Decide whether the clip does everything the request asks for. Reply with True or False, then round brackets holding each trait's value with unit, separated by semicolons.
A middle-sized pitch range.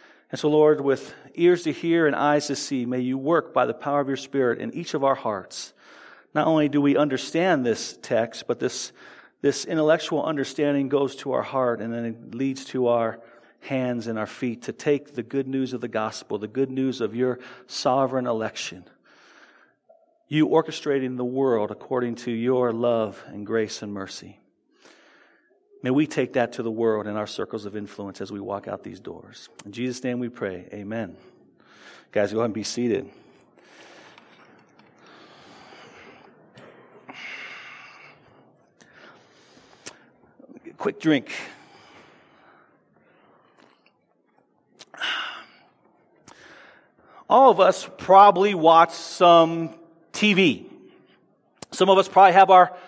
False (5.8 semitones)